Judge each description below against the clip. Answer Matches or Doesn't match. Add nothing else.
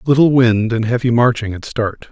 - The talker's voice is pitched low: Matches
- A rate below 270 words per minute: Matches